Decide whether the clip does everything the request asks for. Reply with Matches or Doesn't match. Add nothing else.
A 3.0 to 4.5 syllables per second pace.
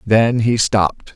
Matches